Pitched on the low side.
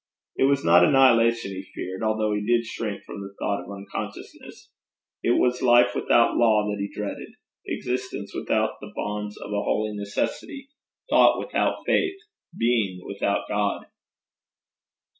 Yes: low, 105 Hz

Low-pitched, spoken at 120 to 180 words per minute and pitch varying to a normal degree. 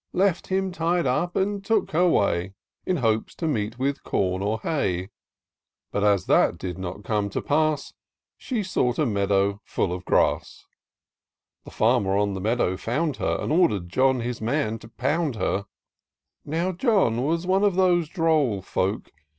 No: low, 125 Hz; average, 165 wpm; wide, 8.9 semitones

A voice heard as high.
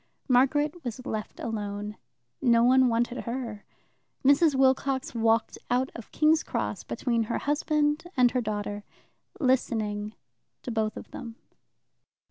Yes: high, 245 Hz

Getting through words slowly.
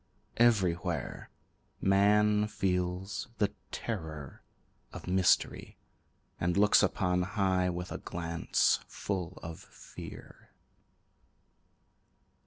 Yes: slow, 80 wpm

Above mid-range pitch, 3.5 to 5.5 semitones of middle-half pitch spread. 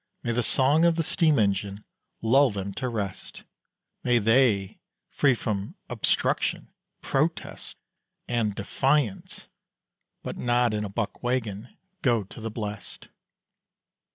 No: low, 115 Hz; average, 4.1 semitones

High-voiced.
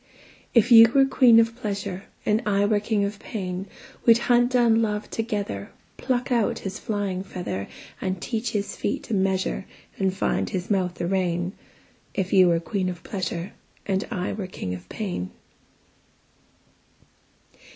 Yes: high, 200 Hz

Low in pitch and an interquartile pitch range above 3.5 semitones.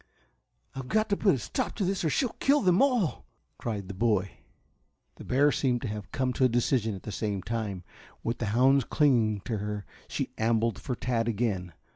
Yes: low, 115 Hz; average, 4.7 semitones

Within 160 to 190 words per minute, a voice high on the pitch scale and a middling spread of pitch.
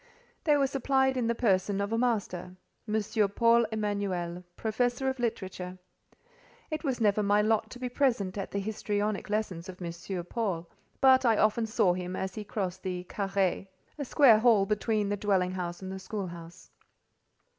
Yes: average, 165 wpm; high, 210 Hz; average, 3.7 semitones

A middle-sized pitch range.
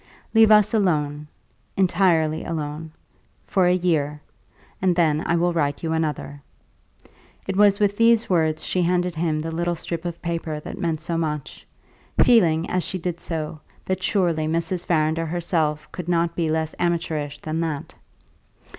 No: narrow, 2.3 semitones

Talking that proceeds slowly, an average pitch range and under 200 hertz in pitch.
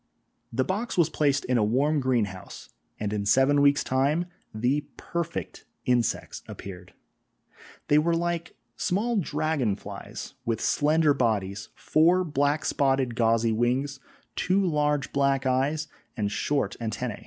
Yes: slow, 130 wpm; average, 4.8 semitones; medium, 140 Hz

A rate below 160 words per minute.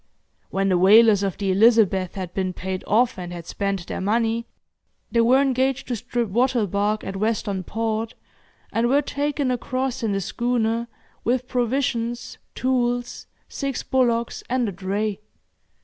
Yes: average, 150 wpm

